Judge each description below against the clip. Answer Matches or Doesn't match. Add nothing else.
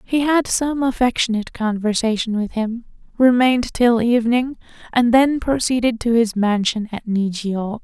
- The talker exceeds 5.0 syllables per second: Doesn't match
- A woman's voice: Matches